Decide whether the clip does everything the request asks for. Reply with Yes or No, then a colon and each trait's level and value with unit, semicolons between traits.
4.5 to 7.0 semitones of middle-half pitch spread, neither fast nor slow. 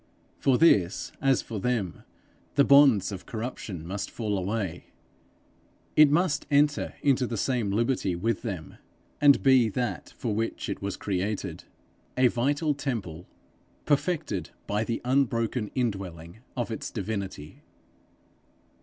No: average, 5.2 semitones; slow, 125 wpm